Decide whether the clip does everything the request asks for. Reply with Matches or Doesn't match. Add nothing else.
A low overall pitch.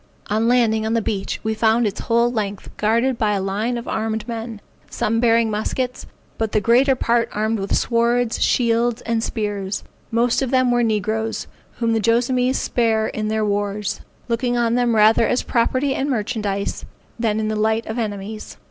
Doesn't match